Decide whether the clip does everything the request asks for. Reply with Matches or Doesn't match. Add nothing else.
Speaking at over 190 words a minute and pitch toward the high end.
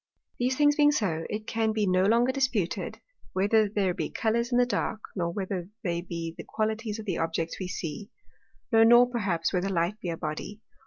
Matches